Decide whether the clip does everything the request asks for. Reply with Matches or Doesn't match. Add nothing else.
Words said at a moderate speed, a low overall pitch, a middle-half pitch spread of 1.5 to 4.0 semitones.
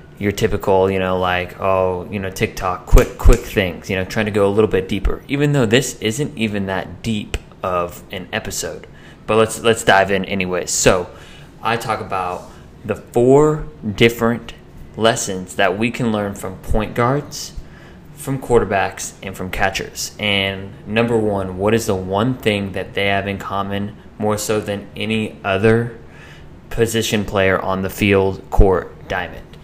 Matches